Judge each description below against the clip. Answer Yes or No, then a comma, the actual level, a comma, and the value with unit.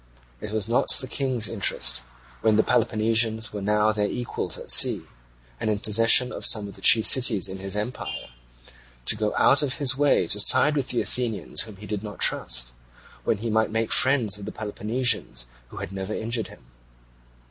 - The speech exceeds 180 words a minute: Yes, average, 190 wpm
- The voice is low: Yes, low, 110 Hz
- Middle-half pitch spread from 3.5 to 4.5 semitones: No, average, 2.7 semitones